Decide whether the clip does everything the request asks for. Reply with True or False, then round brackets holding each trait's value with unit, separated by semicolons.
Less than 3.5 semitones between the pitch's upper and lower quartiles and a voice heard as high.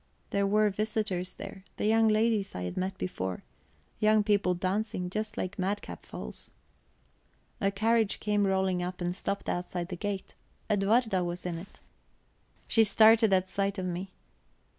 True (2.7 semitones; 195 Hz)